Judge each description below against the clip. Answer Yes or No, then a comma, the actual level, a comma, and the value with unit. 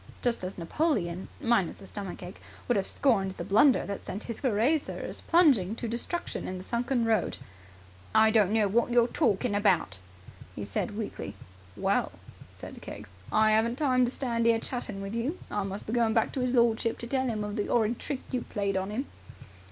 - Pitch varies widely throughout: No, average, 3.5 semitones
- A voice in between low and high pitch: No, high, 225 Hz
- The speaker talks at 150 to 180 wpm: No, average, 195 wpm